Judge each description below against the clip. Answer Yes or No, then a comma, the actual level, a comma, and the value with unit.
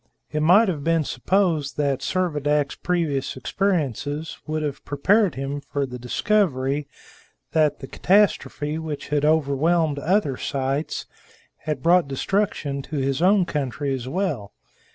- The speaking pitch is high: No, medium, 150 Hz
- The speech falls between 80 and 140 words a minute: Yes, slow, 135 wpm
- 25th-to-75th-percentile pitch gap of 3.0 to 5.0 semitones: Yes, average, 3.9 semitones